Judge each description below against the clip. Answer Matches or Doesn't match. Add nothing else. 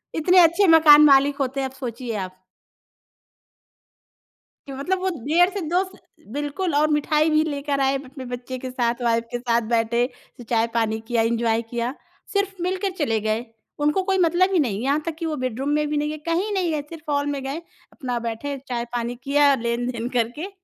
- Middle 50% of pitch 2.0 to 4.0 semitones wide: Doesn't match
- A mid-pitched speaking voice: Doesn't match